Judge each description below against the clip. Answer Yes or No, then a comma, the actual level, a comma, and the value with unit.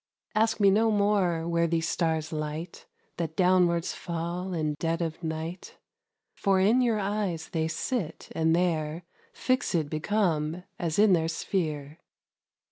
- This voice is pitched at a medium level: Yes, medium, 170 Hz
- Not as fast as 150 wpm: Yes, average, 140 wpm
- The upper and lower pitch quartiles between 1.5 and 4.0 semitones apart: Yes, average, 3.3 semitones